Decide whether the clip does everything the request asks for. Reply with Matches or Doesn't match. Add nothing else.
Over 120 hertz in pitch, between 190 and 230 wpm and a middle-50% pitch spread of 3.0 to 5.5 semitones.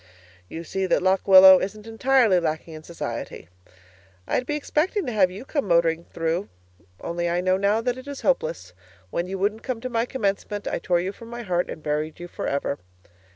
Matches